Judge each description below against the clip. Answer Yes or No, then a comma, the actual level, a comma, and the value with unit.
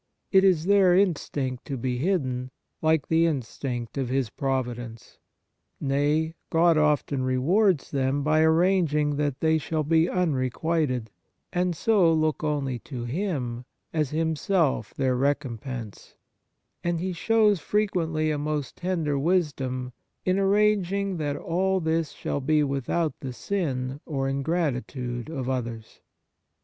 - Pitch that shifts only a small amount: No, average, 4.7 semitones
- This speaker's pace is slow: Yes, slow, 130 wpm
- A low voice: No, medium, 150 Hz